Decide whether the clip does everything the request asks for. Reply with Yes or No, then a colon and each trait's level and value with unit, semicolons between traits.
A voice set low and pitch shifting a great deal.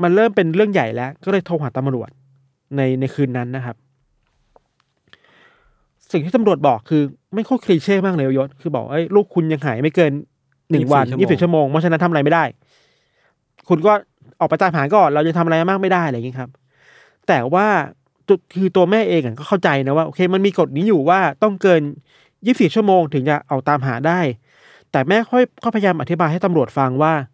No: medium, 160 Hz; wide, 5.7 semitones